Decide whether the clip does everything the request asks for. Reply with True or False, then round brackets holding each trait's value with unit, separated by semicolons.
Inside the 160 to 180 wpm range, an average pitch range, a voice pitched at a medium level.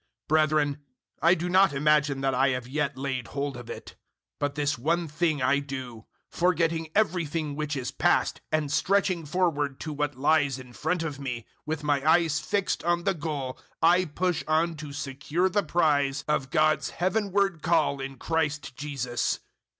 True (175 wpm; 3.3 semitones; 150 Hz)